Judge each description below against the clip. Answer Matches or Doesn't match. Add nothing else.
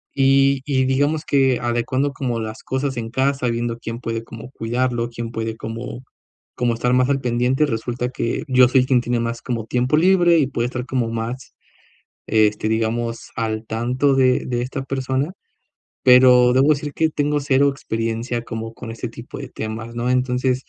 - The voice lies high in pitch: Doesn't match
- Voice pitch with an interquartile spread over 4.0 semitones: Doesn't match